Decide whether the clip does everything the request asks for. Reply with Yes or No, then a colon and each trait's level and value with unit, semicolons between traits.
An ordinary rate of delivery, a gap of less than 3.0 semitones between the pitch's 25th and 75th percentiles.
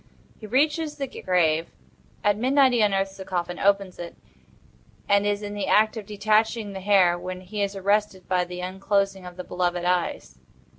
Yes: average, 180 wpm; narrow, 2.6 semitones